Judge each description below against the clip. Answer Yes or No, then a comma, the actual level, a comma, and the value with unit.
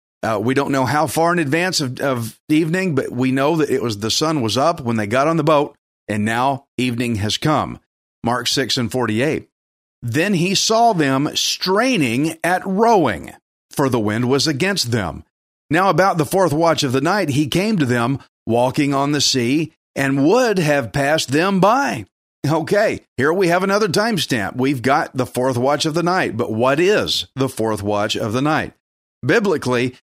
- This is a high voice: No, medium, 140 Hz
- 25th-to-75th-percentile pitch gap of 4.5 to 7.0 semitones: Yes, average, 5.1 semitones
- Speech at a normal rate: Yes, average, 190 wpm